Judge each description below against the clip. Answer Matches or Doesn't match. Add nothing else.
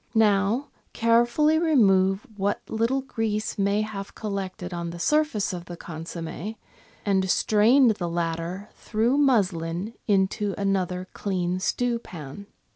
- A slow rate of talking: Matches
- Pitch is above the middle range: Matches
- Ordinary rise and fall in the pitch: Matches